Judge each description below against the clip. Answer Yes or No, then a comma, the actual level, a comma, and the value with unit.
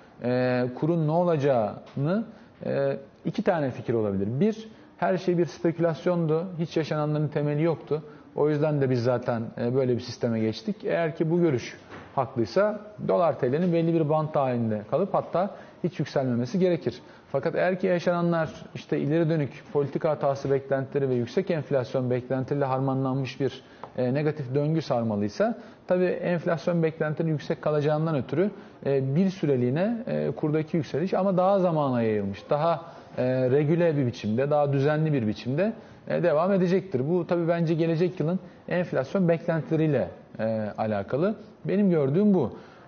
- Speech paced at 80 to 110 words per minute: No, average, 135 wpm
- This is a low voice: No, medium, 155 Hz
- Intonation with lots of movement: No, average, 4.9 semitones